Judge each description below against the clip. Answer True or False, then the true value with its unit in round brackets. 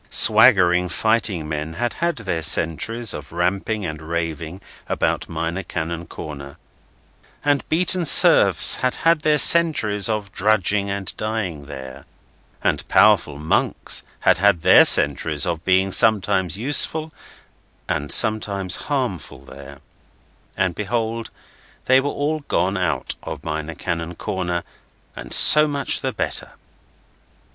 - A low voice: True (95 Hz)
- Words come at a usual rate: False (125 wpm)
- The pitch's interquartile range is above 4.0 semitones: True (5.5 semitones)